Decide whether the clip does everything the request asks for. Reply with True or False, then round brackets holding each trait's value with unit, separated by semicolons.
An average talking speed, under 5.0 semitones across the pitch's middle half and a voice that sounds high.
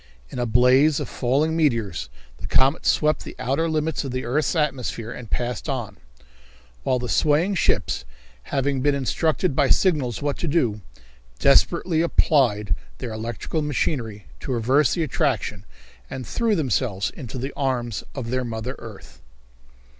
False (150 wpm; 4.4 semitones; 130 Hz)